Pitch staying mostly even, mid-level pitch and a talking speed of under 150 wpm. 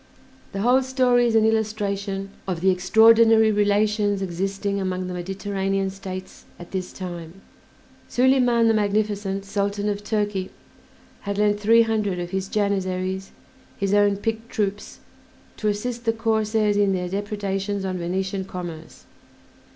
No: narrow, 2.1 semitones; high, 200 Hz; slow, 135 wpm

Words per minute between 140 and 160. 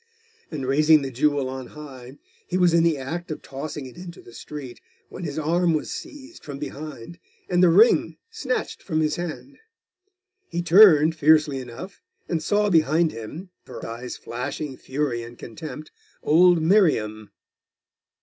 Yes: average, 155 wpm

